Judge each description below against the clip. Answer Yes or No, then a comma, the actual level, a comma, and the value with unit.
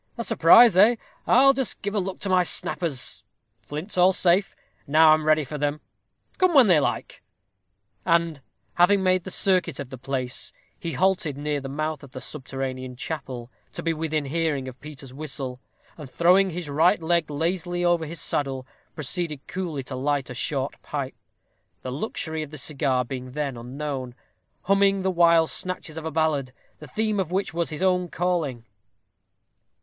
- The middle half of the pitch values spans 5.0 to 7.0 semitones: No, average, 4.6 semitones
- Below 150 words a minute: No, average, 175 wpm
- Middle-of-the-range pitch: Yes, medium, 155 Hz